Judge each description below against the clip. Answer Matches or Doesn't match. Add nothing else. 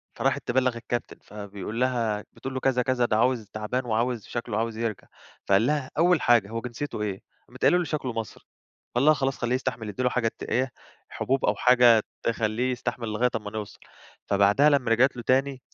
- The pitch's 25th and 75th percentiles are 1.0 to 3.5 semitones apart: Matches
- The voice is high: Doesn't match